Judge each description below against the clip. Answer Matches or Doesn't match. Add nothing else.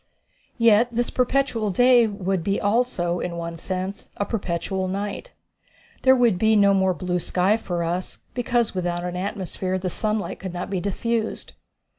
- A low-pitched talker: Doesn't match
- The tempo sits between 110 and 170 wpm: Matches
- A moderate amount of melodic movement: Matches